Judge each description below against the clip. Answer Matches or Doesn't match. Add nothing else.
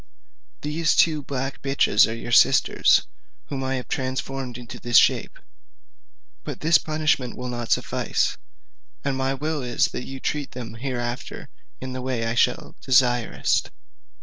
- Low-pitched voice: Matches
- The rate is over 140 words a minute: Matches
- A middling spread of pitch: Doesn't match